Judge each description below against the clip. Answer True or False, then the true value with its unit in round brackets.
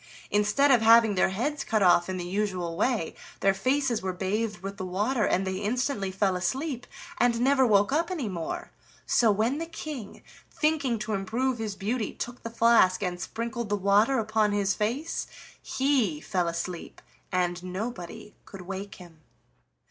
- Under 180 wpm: True (170 wpm)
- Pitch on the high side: True (210 Hz)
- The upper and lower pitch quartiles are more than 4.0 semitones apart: True (4.5 semitones)